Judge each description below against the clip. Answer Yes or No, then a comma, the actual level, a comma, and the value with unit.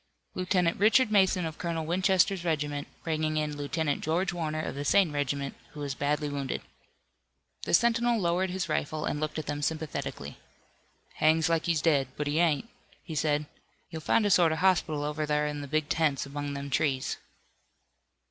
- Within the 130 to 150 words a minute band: No, average, 175 wpm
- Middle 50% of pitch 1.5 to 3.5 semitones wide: Yes, average, 3.0 semitones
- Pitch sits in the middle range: Yes, medium, 155 Hz